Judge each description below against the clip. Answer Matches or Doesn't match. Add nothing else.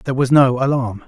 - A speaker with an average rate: Doesn't match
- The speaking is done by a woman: Doesn't match